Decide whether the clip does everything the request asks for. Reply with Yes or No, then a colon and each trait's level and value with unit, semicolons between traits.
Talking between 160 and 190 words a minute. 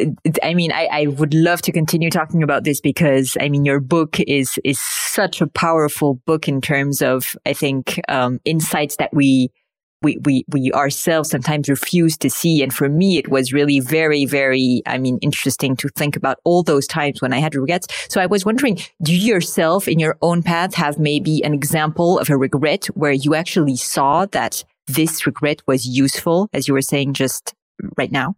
No: average, 200 wpm